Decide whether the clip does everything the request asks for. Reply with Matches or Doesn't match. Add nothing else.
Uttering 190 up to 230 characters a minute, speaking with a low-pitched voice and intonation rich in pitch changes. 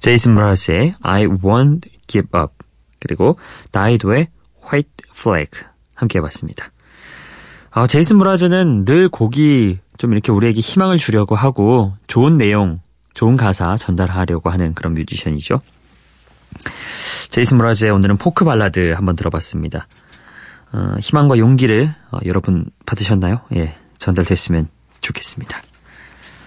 Doesn't match